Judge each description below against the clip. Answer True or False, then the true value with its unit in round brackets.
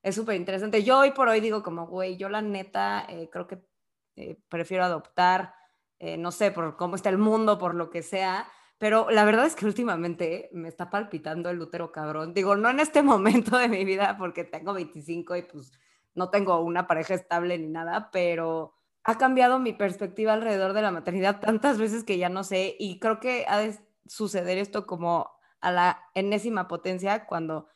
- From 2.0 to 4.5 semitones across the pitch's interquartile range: True (3.8 semitones)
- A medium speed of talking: False (195 wpm)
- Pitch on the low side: False (190 Hz)